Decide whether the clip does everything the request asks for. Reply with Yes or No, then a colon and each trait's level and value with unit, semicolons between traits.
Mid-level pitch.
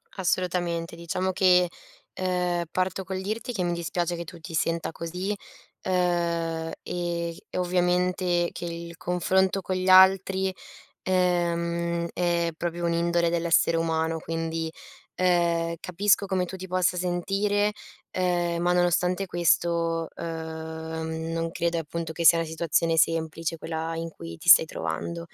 Yes: medium, 170 Hz